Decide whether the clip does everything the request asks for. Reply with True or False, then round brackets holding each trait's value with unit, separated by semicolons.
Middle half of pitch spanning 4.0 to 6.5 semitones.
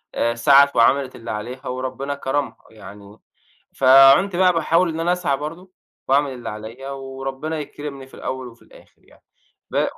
False (2.8 semitones)